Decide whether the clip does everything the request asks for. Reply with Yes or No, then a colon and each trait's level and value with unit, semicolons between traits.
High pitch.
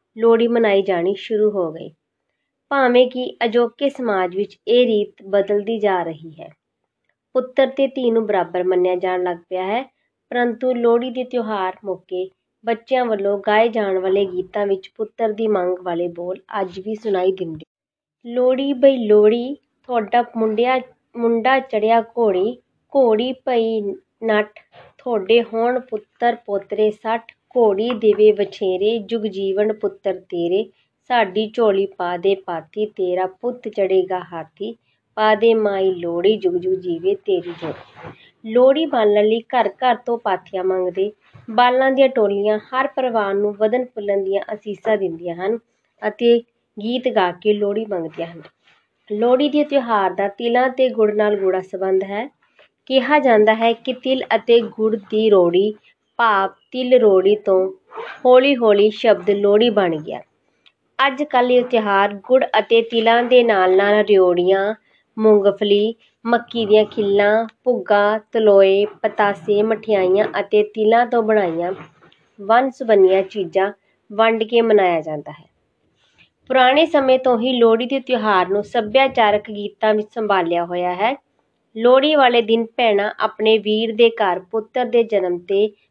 Yes: high, 215 Hz